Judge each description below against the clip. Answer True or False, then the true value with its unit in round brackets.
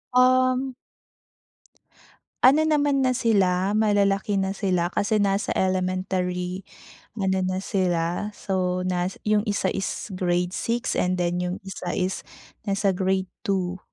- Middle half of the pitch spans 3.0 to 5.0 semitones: False (2.5 semitones)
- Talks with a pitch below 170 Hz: False (190 Hz)